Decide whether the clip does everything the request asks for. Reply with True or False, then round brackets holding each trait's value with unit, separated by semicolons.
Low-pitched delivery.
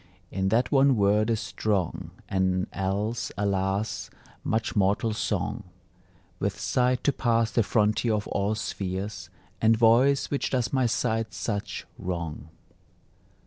True (105 Hz)